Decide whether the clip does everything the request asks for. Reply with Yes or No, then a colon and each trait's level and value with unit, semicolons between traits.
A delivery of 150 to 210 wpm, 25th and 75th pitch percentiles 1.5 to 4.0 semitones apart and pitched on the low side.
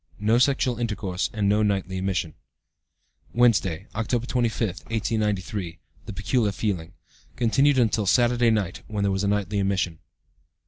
No: slow, 135 wpm; average, 3.3 semitones; low, 105 Hz